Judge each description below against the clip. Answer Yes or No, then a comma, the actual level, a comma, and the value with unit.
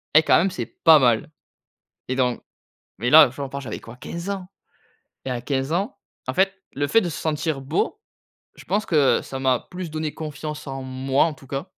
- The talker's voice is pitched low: No, medium, 145 Hz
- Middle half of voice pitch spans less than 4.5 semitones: Yes, average, 3.7 semitones